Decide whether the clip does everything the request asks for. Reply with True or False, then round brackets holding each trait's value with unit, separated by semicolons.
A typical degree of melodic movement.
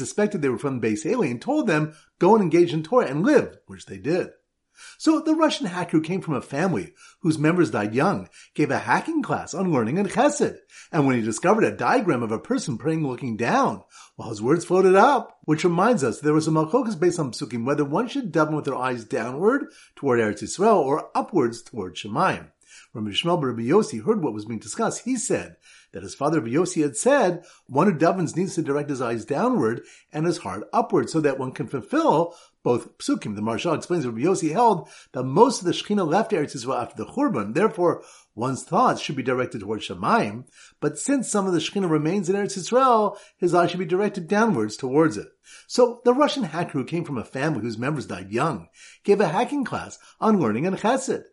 False (6.6 semitones)